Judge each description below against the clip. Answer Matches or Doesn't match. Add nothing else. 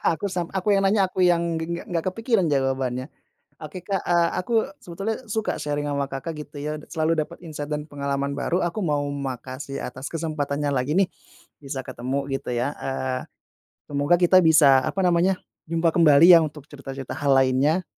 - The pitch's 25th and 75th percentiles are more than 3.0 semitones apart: Matches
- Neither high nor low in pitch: Matches